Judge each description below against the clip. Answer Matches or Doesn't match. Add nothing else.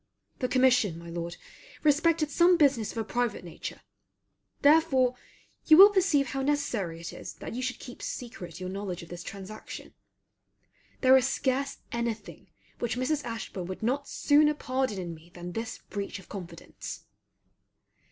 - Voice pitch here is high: Matches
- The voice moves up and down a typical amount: Doesn't match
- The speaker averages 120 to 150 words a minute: Doesn't match